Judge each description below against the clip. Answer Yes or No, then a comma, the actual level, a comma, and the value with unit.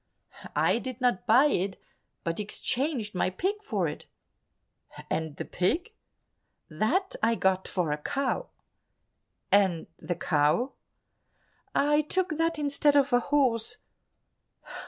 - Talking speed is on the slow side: Yes, slow, 120 wpm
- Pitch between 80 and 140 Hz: No, high, 245 Hz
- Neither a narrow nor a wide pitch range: No, wide, 7.9 semitones